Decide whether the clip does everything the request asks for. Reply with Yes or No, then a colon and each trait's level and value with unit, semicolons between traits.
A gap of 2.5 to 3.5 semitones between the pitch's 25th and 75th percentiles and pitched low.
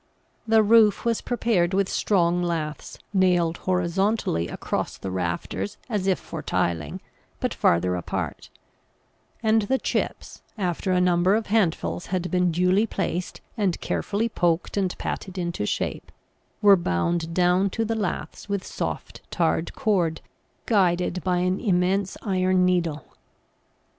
No: average, 2.8 semitones; medium, 180 Hz